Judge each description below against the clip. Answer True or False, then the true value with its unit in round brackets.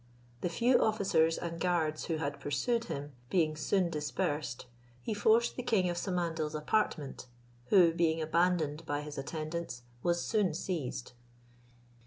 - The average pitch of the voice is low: False (165 Hz)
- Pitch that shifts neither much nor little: True (3.3 semitones)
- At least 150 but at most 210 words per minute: False (140 wpm)